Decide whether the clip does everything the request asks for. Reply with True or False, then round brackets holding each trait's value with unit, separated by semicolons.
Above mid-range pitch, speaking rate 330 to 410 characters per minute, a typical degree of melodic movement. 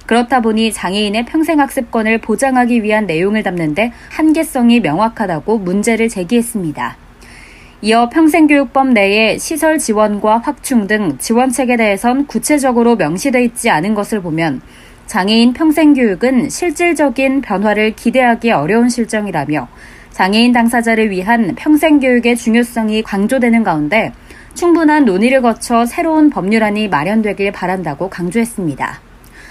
True (230 Hz; 340 characters per minute; 3.7 semitones)